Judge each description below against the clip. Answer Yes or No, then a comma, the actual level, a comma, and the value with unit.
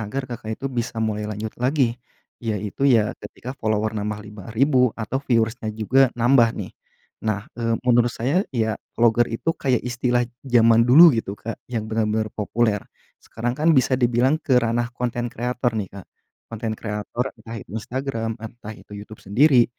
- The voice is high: No, low, 115 Hz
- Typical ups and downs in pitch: No, narrow, 2.3 semitones